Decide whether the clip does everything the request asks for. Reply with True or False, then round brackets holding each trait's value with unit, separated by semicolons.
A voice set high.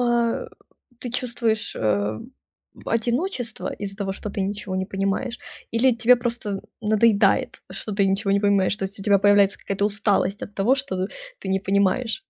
True (205 Hz)